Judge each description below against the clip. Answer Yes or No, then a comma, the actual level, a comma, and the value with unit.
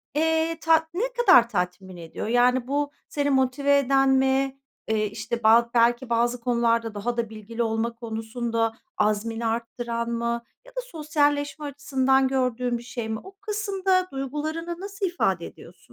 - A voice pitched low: No, high, 245 Hz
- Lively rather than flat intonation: No, average, 4.1 semitones